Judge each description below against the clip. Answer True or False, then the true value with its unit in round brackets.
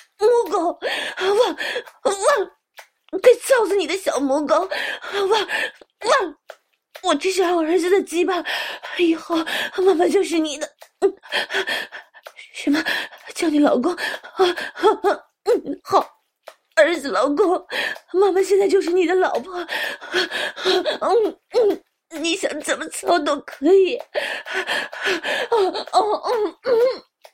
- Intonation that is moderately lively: True (4.0 semitones)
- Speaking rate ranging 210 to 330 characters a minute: False (160 characters per minute)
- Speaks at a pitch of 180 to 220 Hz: False (370 Hz)